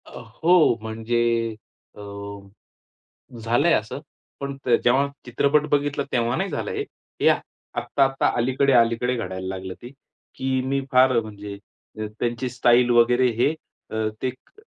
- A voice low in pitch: Yes, low, 125 Hz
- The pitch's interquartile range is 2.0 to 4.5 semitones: Yes, average, 2.9 semitones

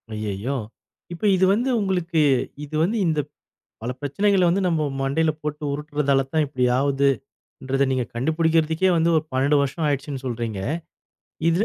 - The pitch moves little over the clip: No, average, 3.4 semitones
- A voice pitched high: No, medium, 150 Hz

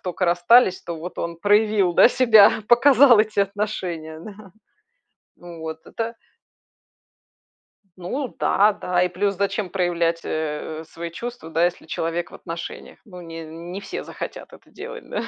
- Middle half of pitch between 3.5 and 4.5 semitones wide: Yes, average, 3.9 semitones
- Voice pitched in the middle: Yes, medium, 180 Hz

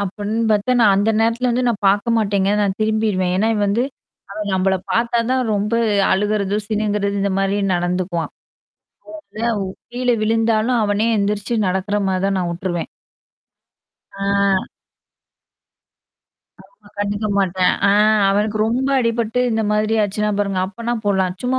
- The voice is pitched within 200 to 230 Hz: Yes, high, 205 Hz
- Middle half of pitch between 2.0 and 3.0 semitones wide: Yes, narrow, 2.4 semitones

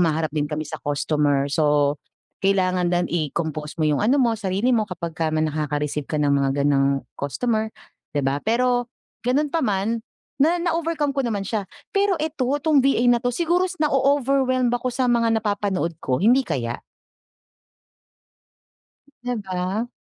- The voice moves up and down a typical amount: No, wide, 8.8 semitones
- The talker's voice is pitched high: Yes, high, 205 Hz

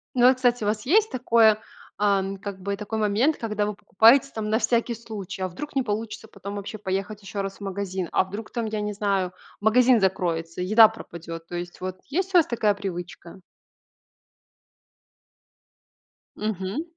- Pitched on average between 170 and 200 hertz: No, high, 210 Hz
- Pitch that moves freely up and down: No, average, 3.0 semitones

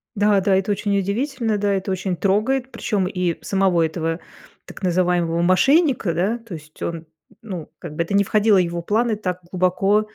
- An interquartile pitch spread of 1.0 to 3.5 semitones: Yes, average, 3.2 semitones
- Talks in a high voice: Yes, high, 195 Hz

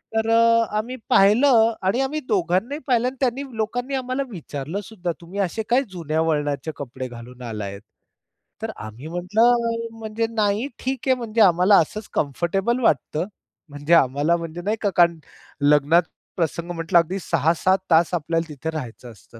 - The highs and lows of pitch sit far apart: Yes, wide, 6.4 semitones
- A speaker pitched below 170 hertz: No, medium, 180 Hz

